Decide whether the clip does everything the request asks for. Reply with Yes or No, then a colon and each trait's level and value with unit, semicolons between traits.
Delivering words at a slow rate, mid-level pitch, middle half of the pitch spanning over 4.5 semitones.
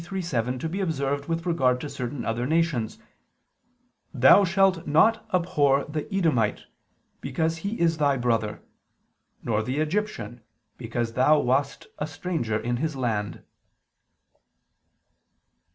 Yes: slow, 120 wpm; medium, 145 Hz; wide, 5.4 semitones